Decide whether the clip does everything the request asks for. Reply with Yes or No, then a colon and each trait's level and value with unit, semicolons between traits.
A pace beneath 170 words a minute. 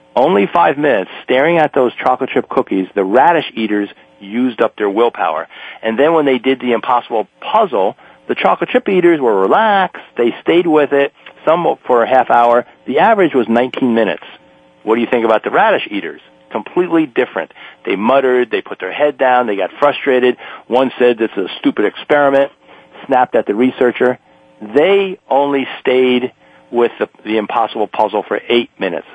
No: average, 175 wpm